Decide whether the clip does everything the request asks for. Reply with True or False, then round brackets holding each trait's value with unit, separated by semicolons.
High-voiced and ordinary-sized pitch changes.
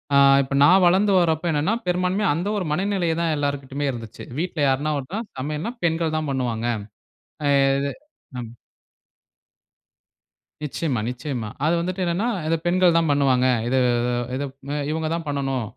False (155 Hz; 4.5 semitones)